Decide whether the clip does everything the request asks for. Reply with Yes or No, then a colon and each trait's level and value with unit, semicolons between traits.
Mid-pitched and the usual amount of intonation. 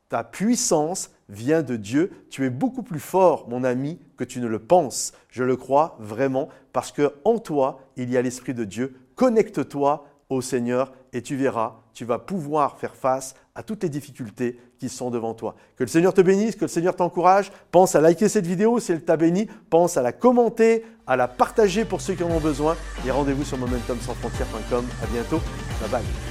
No: medium, 145 Hz; wide, 6.4 semitones